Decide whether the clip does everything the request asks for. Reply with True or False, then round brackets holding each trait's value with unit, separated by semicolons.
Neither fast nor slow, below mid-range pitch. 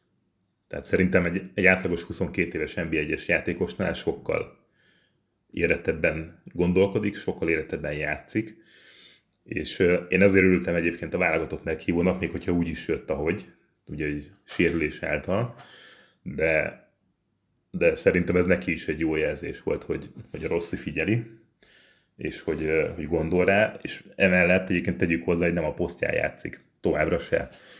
True (145 wpm; 90 Hz)